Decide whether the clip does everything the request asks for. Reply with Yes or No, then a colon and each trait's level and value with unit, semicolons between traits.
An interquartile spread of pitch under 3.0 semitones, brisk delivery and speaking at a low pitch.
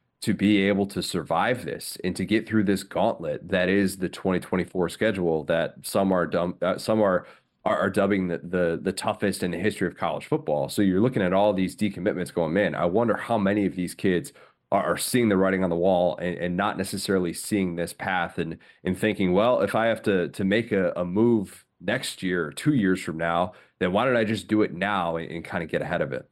Yes: narrow, 2.6 semitones; fast, 235 wpm; very low, 95 Hz